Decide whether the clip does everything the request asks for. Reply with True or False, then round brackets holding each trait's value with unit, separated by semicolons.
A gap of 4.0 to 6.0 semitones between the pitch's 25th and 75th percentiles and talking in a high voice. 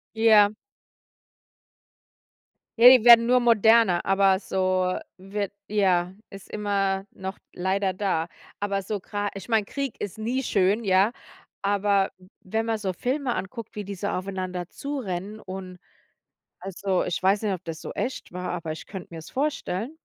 False (2.9 semitones; 200 Hz)